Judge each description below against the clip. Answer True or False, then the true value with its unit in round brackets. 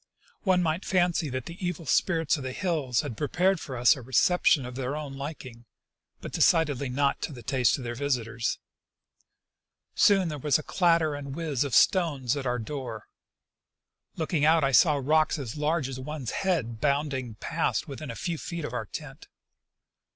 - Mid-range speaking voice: True (145 Hz)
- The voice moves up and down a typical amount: True (4.0 semitones)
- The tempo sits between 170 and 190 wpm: True (180 wpm)